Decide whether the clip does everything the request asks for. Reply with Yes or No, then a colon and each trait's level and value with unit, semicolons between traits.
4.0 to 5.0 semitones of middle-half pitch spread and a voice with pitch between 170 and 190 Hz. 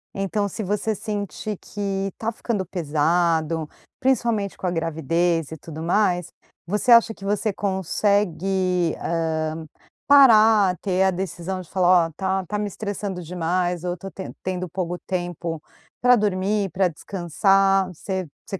No: average, 2.9 semitones; medium, 185 Hz